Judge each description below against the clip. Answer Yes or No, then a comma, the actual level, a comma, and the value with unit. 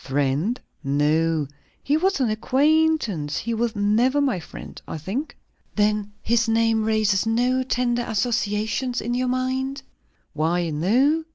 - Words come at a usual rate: No, slow, 130 wpm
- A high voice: Yes, high, 225 Hz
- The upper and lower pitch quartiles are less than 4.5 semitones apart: No, average, 4.8 semitones